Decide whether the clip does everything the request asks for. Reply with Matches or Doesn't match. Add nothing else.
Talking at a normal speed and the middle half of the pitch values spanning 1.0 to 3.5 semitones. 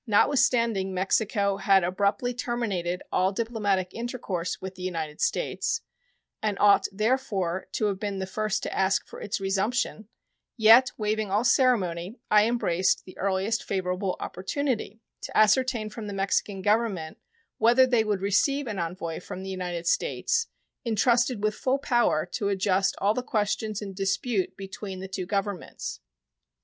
Matches